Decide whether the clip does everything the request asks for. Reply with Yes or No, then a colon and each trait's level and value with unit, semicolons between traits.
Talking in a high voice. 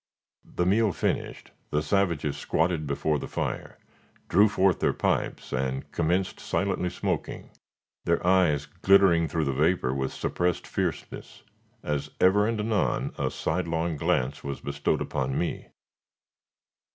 No: very low, 85 Hz